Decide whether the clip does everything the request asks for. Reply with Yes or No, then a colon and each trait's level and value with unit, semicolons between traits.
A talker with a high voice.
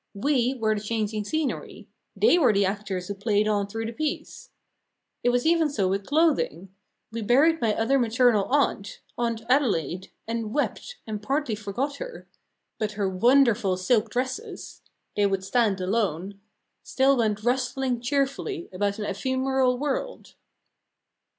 Yes: high, 230 Hz